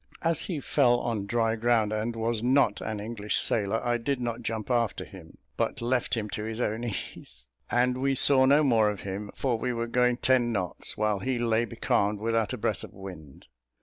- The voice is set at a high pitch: No, low, 115 Hz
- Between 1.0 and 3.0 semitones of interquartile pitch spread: Yes, narrow, 2.6 semitones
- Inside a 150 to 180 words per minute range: No, fast, 205 wpm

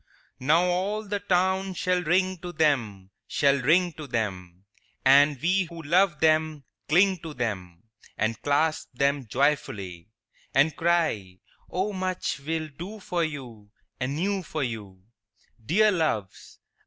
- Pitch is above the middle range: No, medium, 155 Hz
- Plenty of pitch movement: Yes, wide, 6.7 semitones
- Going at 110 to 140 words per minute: Yes, slow, 135 wpm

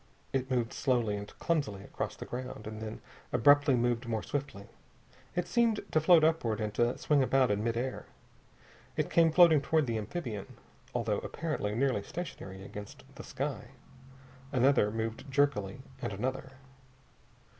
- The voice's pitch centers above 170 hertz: No, low, 125 Hz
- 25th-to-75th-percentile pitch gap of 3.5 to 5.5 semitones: Yes, average, 5.0 semitones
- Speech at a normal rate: Yes, average, 150 wpm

